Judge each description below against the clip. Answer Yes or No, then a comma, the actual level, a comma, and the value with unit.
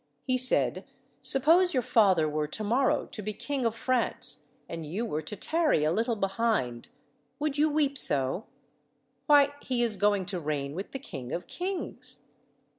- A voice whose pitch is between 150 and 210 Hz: No, high, 225 Hz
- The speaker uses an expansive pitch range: Yes, wide, 8.4 semitones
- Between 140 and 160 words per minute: No, average, 170 wpm